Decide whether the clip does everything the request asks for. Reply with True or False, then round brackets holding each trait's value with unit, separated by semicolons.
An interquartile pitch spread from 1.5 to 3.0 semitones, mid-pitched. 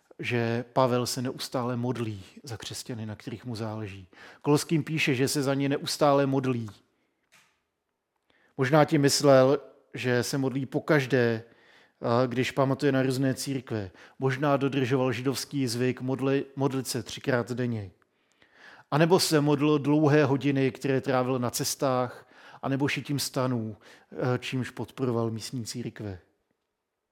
False (2.5 semitones; 130 Hz)